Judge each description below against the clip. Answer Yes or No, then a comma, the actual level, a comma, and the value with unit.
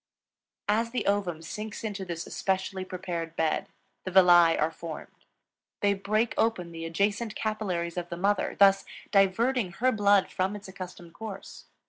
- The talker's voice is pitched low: No, high, 190 Hz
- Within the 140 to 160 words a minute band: Yes, average, 150 wpm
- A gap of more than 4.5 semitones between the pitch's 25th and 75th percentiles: No, average, 3.1 semitones